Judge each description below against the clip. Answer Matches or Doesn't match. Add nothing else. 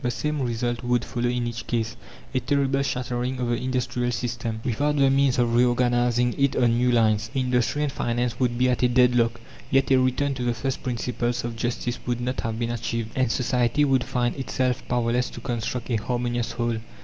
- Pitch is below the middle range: Matches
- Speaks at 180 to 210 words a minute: Matches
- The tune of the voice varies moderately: Doesn't match